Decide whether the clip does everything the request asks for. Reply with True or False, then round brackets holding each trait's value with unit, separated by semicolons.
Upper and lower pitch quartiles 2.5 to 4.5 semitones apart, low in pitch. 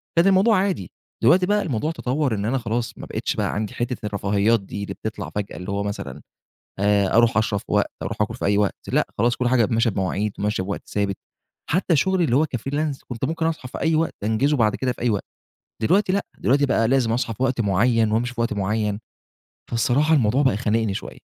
False (5.2 semitones; 115 Hz)